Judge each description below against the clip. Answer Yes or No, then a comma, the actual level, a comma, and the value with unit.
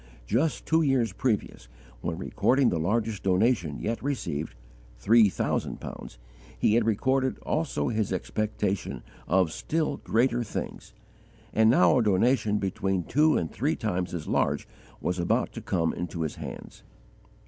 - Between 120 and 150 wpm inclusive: Yes, average, 145 wpm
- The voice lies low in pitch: Yes, low, 105 Hz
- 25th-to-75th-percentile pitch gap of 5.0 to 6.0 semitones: Yes, average, 5.3 semitones